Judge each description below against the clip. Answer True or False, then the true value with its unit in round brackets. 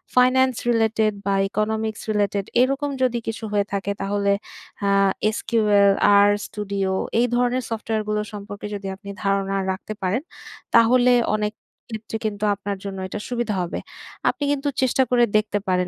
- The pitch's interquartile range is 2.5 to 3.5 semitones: True (2.9 semitones)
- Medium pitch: False (215 Hz)